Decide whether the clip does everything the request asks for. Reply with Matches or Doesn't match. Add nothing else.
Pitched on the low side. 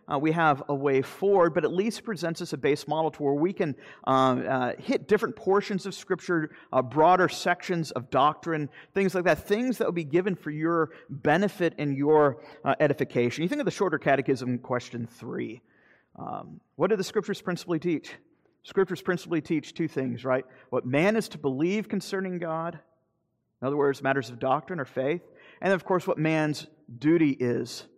Doesn't match